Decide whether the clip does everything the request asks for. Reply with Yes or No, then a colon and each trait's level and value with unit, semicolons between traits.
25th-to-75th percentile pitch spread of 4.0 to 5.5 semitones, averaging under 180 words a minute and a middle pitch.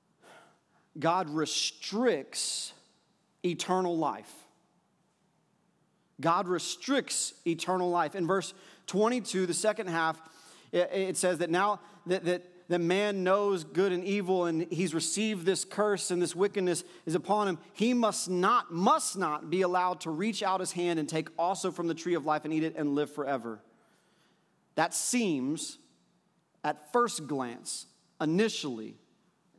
No: average, 3.0 semitones; average, 140 wpm; medium, 180 Hz